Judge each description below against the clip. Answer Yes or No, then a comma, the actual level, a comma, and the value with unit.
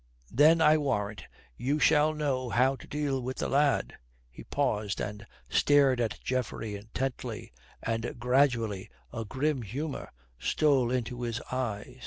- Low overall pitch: Yes, low, 130 Hz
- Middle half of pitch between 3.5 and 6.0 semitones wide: Yes, average, 4.0 semitones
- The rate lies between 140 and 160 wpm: Yes, average, 145 wpm